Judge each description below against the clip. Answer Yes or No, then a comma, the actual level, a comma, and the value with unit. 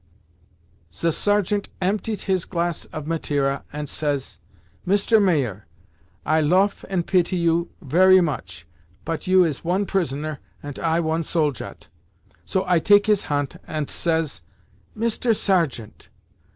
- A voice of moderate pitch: Yes, medium, 170 Hz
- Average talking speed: No, slow, 130 wpm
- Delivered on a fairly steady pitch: No, average, 4.1 semitones